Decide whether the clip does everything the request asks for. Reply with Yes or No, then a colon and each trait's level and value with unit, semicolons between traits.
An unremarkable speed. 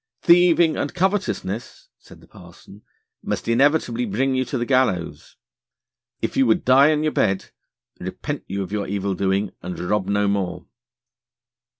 Yes: average, 150 wpm